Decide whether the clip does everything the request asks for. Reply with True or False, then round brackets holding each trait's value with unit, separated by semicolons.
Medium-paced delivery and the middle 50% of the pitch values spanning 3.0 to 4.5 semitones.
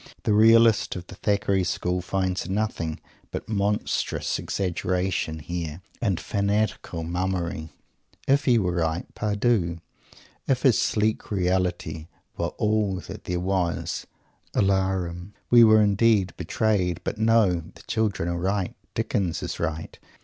False (130 wpm; 3.4 semitones)